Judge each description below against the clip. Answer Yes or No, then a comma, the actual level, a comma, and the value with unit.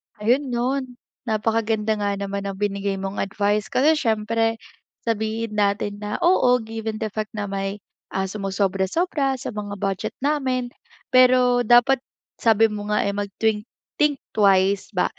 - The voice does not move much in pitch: No, average, 3.2 semitones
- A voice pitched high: Yes, high, 215 Hz